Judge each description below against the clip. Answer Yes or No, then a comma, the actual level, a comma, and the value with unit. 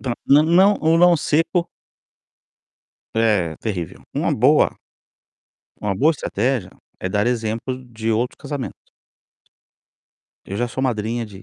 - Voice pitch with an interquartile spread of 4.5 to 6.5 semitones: Yes, average, 5.2 semitones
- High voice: No, low, 120 Hz